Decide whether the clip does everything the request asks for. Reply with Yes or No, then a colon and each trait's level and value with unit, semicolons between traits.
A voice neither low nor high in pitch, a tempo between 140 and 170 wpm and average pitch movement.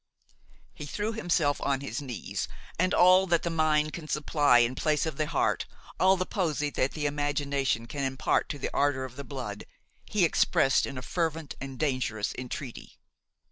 No: medium, 145 Hz; average, 180 wpm; average, 3.5 semitones